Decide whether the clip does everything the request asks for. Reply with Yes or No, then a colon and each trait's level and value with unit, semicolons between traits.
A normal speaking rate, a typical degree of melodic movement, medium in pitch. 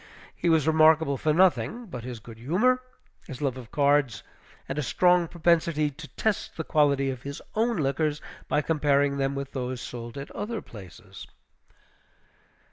Yes: average, 160 wpm; average, 3.5 semitones; medium, 145 Hz